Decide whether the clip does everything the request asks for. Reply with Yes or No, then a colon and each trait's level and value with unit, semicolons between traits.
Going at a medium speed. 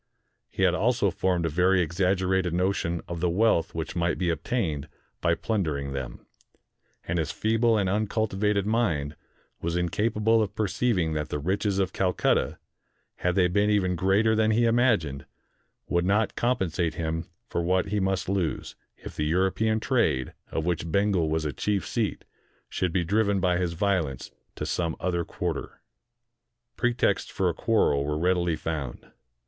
Yes: average, 165 wpm